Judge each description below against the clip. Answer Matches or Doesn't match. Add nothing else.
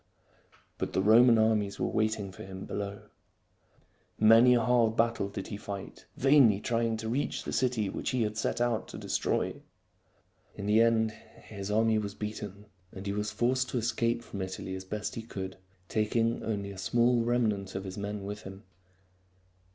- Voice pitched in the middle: Doesn't match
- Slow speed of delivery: Doesn't match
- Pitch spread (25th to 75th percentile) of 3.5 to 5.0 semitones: Doesn't match